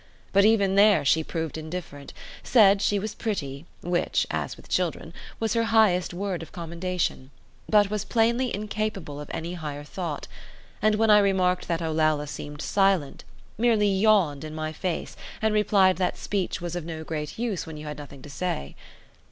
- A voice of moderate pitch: Yes, medium, 180 Hz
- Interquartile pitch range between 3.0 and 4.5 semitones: No, average, 4.9 semitones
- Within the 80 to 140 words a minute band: No, average, 175 wpm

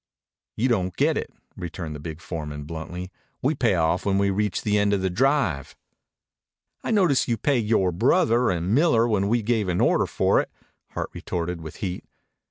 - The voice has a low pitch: Yes, low, 100 Hz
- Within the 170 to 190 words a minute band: Yes, average, 185 wpm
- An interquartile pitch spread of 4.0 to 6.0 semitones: Yes, average, 5.3 semitones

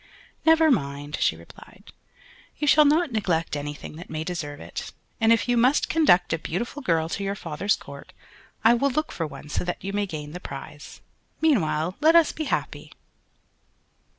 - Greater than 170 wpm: Yes, average, 180 wpm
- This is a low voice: No, medium, 185 Hz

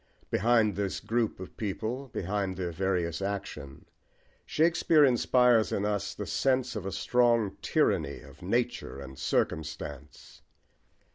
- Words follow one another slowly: Yes, slow, 125 wpm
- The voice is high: No, low, 100 Hz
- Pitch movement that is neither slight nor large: Yes, average, 5.0 semitones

